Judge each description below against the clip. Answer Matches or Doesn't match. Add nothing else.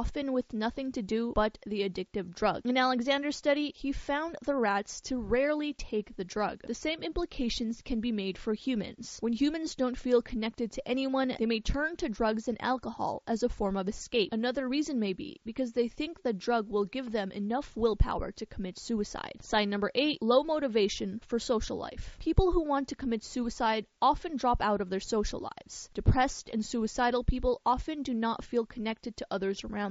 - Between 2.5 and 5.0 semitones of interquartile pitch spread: Matches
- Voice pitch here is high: Matches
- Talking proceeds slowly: Doesn't match